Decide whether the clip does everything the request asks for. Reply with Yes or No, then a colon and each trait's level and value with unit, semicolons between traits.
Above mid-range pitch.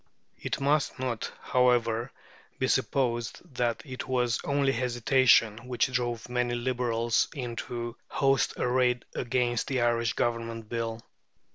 No: low, 120 Hz